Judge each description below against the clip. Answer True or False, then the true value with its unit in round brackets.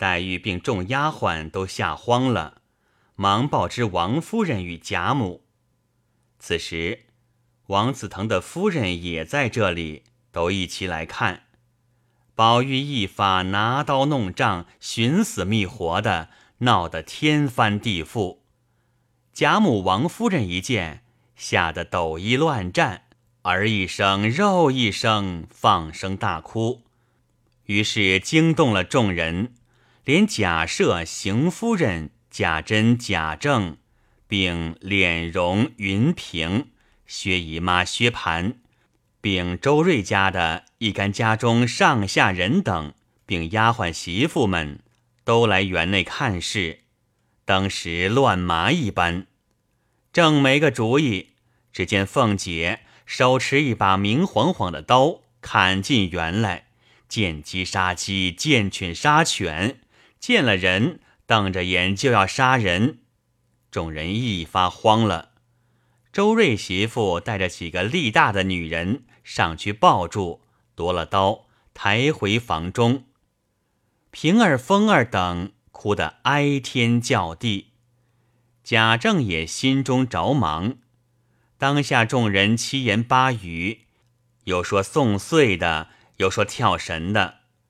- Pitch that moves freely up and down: False (4.8 semitones)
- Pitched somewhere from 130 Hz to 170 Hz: False (110 Hz)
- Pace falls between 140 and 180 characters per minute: True (165 characters per minute)